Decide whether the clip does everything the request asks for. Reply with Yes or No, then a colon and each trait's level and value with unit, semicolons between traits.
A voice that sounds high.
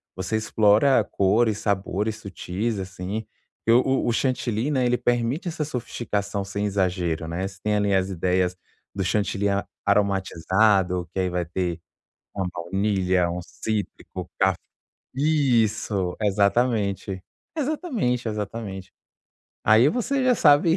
No: low, 100 Hz